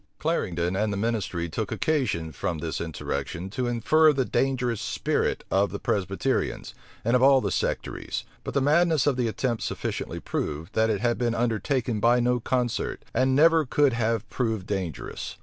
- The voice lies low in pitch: Yes, low, 115 Hz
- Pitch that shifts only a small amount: No, average, 4.7 semitones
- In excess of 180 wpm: No, average, 170 wpm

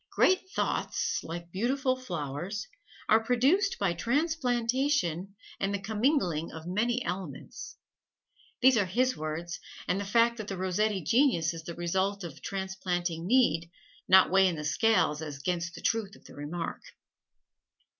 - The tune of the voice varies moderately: No, wide, 5.7 semitones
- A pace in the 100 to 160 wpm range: Yes, average, 145 wpm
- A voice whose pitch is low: No, high, 195 Hz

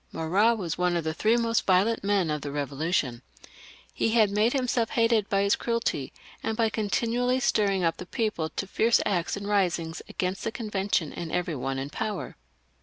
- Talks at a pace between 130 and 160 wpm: No, average, 185 wpm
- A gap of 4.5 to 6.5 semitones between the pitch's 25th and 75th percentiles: Yes, average, 5.2 semitones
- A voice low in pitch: No, high, 200 Hz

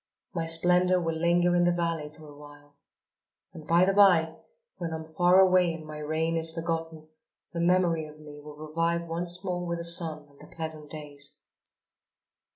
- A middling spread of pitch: No, narrow, 2.2 semitones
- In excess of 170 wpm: Yes, average, 185 wpm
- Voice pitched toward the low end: No, medium, 165 Hz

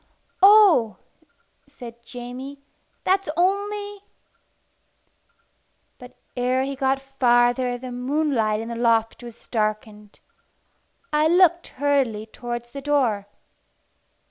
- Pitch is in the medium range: No, very high, 250 Hz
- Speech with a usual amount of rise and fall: Yes, average, 3.8 semitones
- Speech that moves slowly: Yes, slow, 100 wpm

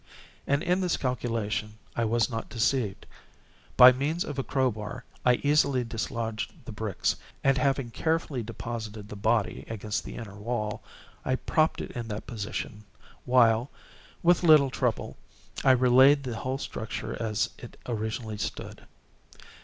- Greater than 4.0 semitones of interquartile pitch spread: No, average, 3.5 semitones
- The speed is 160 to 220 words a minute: No, average, 150 wpm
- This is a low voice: Yes, low, 120 Hz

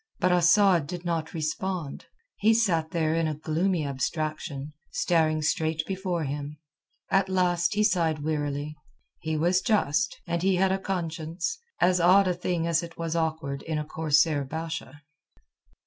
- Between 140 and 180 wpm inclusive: Yes, average, 155 wpm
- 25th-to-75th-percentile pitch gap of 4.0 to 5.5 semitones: No, average, 2.9 semitones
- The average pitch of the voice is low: No, medium, 165 Hz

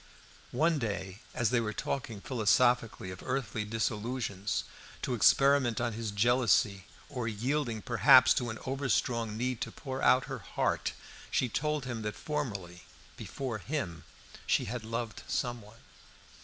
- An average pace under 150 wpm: Yes, average, 140 wpm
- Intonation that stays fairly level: No, average, 3.3 semitones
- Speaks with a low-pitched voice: Yes, low, 115 Hz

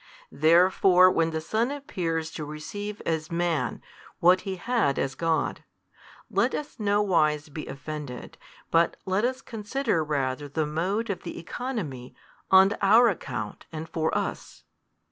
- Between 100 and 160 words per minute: Yes, average, 145 wpm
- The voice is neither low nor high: Yes, medium, 170 Hz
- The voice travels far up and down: No, average, 4.9 semitones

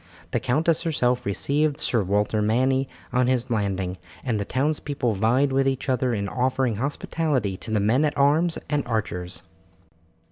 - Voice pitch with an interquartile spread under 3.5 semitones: No, average, 4.7 semitones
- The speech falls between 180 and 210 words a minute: No, average, 155 wpm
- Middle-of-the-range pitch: No, low, 125 Hz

